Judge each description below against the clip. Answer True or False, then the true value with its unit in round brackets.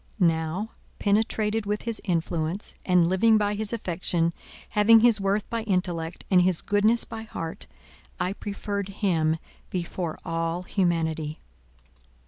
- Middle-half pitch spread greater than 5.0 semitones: False (4.0 semitones)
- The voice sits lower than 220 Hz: True (190 Hz)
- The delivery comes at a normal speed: False (120 wpm)